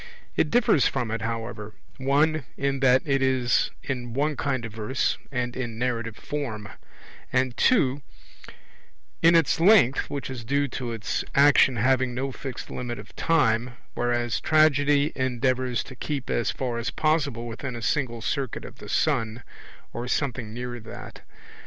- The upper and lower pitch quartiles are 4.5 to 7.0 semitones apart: No, average, 3.1 semitones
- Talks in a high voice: No, low, 130 Hz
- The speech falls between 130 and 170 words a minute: Yes, average, 155 wpm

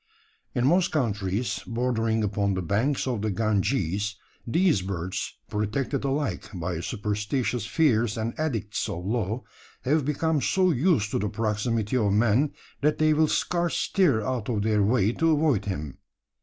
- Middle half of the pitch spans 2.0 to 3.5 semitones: No, average, 5.2 semitones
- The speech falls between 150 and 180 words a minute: Yes, average, 155 wpm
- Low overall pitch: Yes, low, 115 Hz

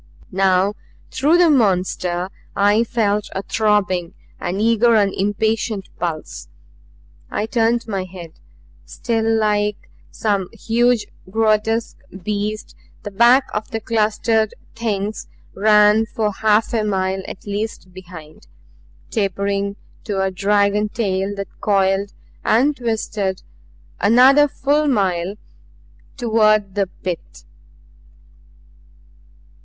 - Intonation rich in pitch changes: No, narrow, 2.6 semitones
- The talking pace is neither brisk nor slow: No, slow, 105 wpm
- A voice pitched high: Yes, high, 210 Hz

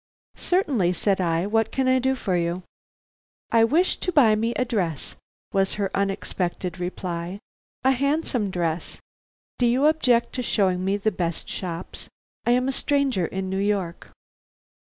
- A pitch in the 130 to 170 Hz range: No, high, 200 Hz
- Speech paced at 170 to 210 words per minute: No, average, 155 wpm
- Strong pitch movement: Yes, wide, 5.8 semitones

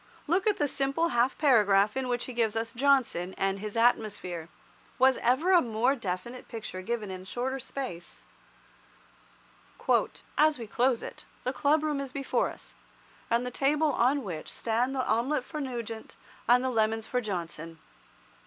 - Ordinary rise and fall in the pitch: Yes, average, 4.0 semitones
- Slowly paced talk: No, average, 165 wpm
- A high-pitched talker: Yes, high, 245 Hz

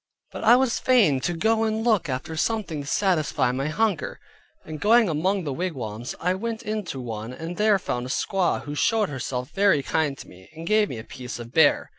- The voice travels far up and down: Yes, wide, 8.1 semitones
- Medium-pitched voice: Yes, medium, 165 Hz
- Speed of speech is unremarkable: No, fast, 210 wpm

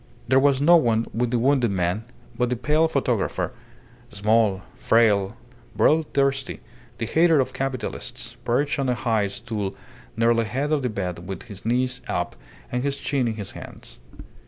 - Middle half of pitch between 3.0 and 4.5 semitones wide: Yes, average, 3.9 semitones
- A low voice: Yes, low, 120 Hz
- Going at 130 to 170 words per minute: Yes, average, 165 wpm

